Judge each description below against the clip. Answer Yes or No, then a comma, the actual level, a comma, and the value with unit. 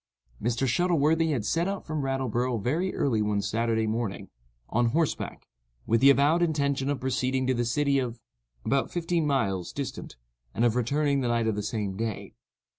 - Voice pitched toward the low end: Yes, low, 125 Hz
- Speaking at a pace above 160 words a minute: Yes, average, 180 wpm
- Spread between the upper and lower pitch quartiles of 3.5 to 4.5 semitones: Yes, average, 4.2 semitones